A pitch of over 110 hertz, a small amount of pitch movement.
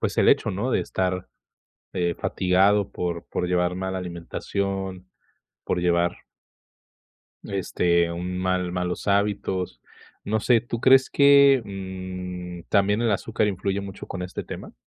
No: very low, 95 Hz; narrow, 2.2 semitones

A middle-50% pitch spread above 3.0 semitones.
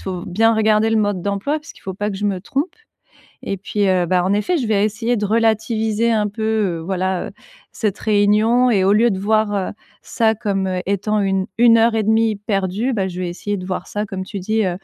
No: narrow, 2.5 semitones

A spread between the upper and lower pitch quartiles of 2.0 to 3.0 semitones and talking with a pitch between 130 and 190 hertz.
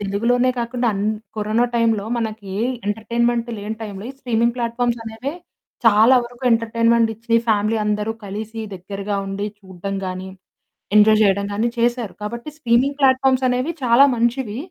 No: narrow, 2.4 semitones; high, 225 Hz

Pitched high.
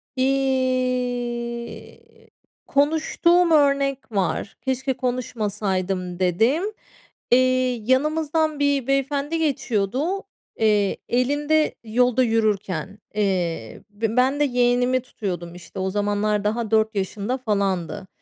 Yes: high, 245 Hz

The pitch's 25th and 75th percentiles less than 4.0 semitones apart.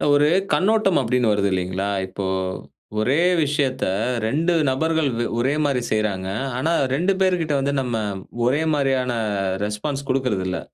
No: wide, 5.5 semitones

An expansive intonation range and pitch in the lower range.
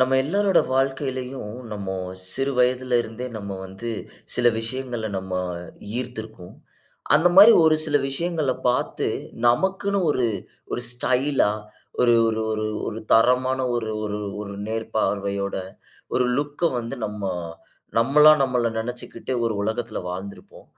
No: average, 3.6 semitones; low, 125 Hz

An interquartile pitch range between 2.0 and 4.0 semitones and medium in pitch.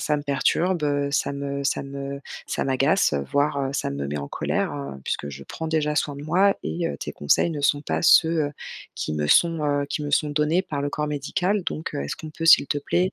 Yes: narrow, 2.4 semitones; medium, 145 Hz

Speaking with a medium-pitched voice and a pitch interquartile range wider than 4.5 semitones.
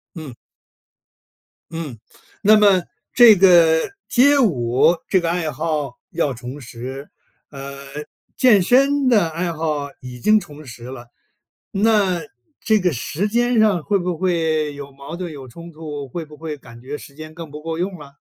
Yes: medium, 160 Hz; average, 5.2 semitones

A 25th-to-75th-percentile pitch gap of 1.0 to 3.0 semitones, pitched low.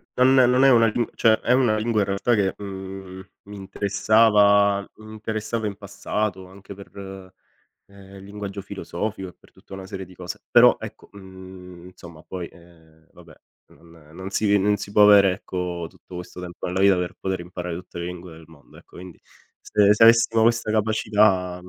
Yes: narrow, 2.6 semitones; very low, 95 Hz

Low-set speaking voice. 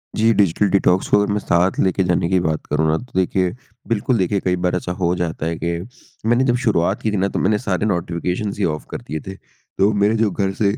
Yes: very low, 95 Hz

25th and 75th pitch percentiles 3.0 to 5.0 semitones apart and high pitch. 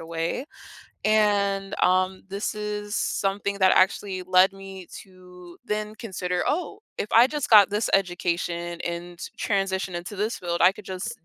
No: narrow, 2.4 semitones; high, 195 Hz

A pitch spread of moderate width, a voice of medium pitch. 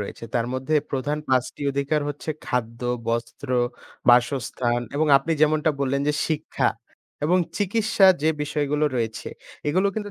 Yes: average, 4.1 semitones; medium, 145 Hz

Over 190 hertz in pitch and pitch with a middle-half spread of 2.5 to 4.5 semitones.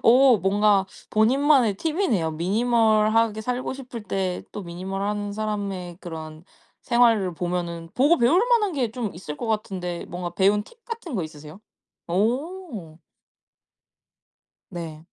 No: high, 210 Hz; wide, 5.5 semitones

